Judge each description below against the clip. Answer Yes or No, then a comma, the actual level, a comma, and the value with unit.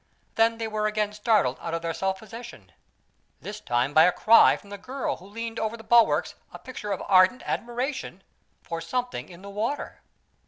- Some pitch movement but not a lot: Yes, average, 3.7 semitones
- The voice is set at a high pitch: Yes, high, 215 Hz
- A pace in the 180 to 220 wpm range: Yes, average, 190 wpm